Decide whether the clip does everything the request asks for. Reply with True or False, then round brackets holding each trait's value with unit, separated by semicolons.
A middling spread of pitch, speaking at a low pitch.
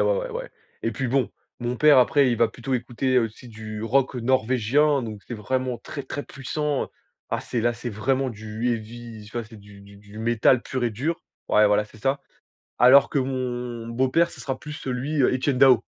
True (3.1 semitones; 125 Hz)